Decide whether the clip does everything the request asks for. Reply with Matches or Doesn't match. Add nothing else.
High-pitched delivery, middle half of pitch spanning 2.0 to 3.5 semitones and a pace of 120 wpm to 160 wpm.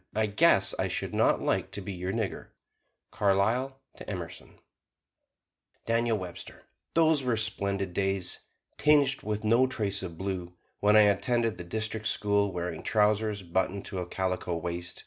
Doesn't match